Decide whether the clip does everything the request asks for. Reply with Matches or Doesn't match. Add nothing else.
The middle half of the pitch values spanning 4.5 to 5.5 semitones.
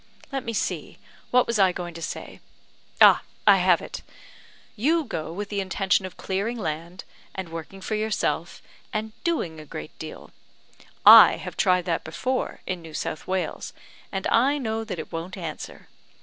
Matches